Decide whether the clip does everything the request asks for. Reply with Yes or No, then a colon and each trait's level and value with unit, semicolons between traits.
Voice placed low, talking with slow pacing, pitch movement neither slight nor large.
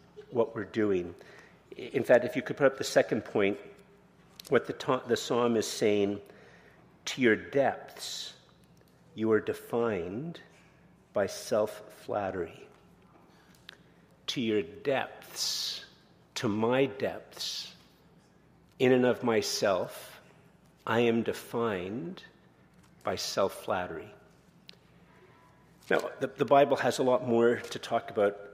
Yes: low, 120 Hz; slow, 120 wpm; average, 3.2 semitones